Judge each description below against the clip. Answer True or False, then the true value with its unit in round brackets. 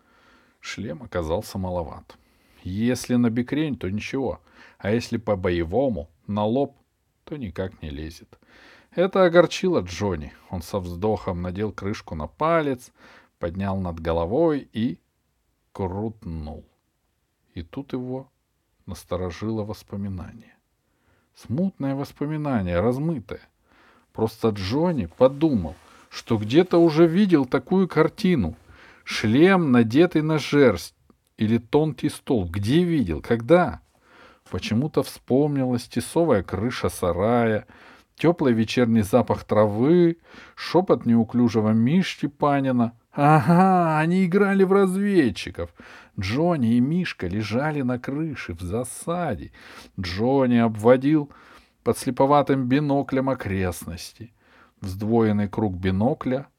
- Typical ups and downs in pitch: False (6.3 semitones)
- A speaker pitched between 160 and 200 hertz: False (120 Hz)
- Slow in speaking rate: True (100 wpm)